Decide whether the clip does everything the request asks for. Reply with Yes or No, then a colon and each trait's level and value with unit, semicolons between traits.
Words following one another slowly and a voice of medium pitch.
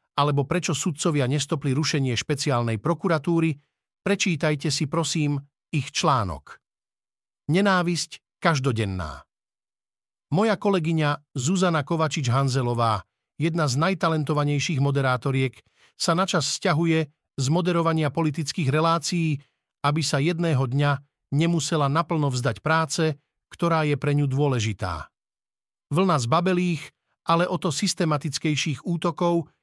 Yes: slow, 100 wpm; medium, 155 Hz